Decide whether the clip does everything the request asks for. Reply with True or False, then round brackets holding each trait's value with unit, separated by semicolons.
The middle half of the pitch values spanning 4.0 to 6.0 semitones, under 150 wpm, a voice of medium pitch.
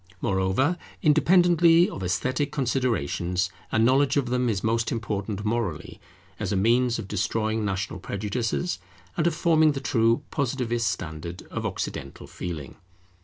False (5.6 semitones; 135 wpm; 115 Hz)